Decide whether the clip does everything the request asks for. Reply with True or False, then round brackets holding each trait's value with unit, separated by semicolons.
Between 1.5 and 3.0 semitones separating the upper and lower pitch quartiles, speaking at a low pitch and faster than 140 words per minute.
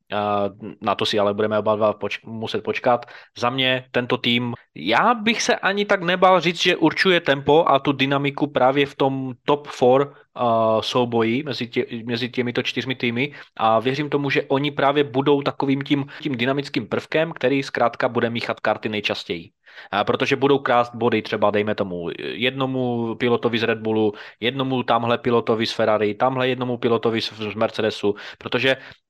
False (3.5 semitones; 125 Hz; 170 wpm)